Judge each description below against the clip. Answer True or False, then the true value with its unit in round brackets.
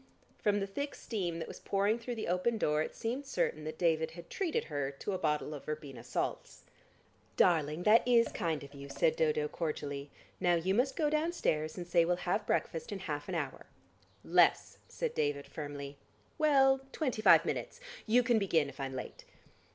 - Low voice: False (175 Hz)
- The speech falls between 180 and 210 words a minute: True (190 wpm)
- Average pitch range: False (7.5 semitones)